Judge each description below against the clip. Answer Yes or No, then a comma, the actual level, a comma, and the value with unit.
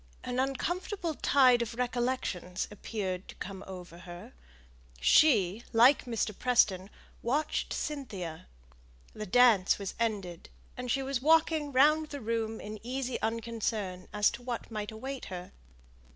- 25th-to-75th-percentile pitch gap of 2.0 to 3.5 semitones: No, average, 4.9 semitones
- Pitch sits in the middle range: No, high, 230 Hz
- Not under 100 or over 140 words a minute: Yes, slow, 135 wpm